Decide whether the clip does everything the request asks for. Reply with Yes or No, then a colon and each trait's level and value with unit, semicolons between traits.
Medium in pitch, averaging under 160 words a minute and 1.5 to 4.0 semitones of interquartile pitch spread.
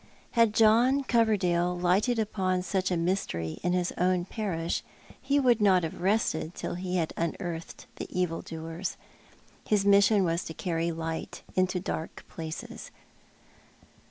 Yes: medium, 180 Hz; average, 140 wpm; average, 3.6 semitones